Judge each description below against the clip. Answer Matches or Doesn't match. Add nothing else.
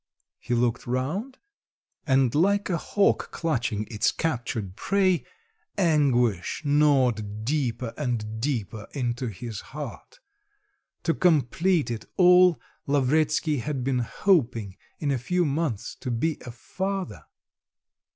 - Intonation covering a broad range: Matches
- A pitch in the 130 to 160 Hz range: Matches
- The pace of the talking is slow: Matches